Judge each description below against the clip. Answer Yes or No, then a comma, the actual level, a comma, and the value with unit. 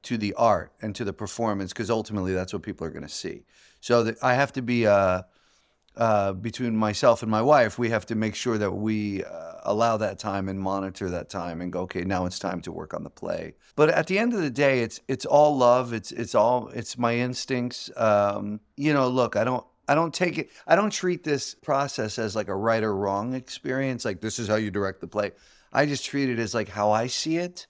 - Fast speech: Yes, fast, 245 wpm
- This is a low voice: Yes, low, 115 Hz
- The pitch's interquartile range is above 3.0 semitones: Yes, average, 4.0 semitones